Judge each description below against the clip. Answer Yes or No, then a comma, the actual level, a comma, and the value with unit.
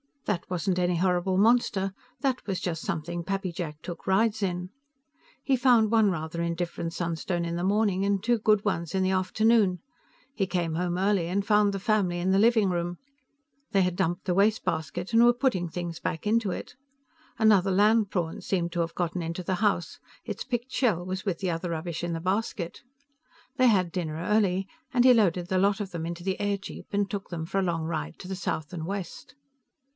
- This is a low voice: No, medium, 185 Hz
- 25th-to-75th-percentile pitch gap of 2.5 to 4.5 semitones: Yes, average, 3.1 semitones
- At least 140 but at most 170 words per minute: No, average, 200 wpm